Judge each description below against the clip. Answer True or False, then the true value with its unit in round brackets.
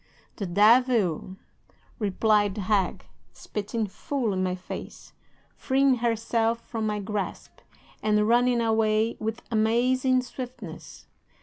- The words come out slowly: True (110 wpm)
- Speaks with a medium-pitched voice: False (220 Hz)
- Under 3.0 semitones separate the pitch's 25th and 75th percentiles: True (2.6 semitones)